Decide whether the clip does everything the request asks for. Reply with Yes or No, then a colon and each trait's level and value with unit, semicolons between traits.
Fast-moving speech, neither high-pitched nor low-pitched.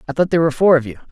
Yes: fast, 375 wpm; medium, 155 Hz